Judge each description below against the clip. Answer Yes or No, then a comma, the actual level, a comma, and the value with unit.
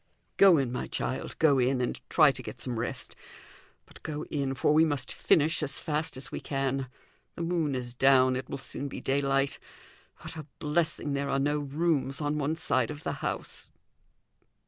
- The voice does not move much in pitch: Yes, narrow, 2.3 semitones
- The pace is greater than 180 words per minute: Yes, average, 190 wpm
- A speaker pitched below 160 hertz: Yes, medium, 140 Hz